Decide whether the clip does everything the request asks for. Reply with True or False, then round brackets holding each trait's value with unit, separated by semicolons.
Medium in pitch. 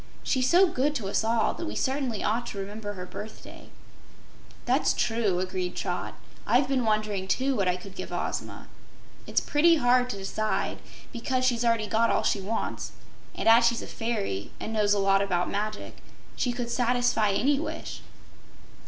False (225 Hz)